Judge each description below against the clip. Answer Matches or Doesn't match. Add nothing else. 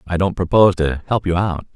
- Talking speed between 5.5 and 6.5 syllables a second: Matches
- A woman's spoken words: Doesn't match